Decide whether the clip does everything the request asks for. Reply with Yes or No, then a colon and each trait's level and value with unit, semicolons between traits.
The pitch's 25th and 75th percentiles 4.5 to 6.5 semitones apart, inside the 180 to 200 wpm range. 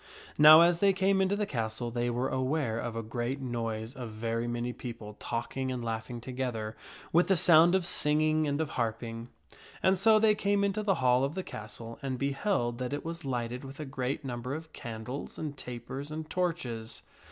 Yes: average, 5.1 semitones; average, 195 wpm